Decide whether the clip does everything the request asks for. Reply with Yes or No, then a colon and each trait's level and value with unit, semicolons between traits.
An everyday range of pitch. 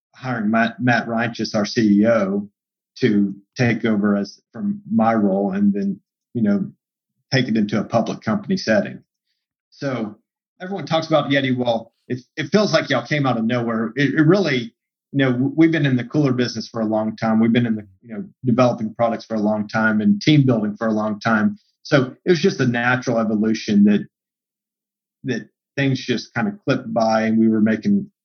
No: wide, 6.8 semitones